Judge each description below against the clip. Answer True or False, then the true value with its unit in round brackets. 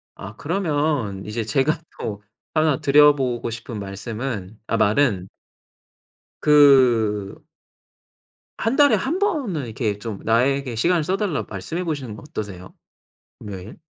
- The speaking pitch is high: False (125 Hz)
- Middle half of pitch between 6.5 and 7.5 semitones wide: False (6.0 semitones)